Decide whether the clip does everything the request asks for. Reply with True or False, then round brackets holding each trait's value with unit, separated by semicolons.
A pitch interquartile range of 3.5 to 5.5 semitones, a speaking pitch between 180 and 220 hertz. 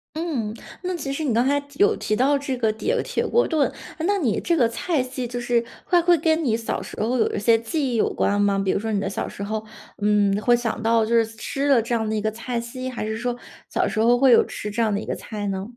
False (4.2 semitones; 235 Hz)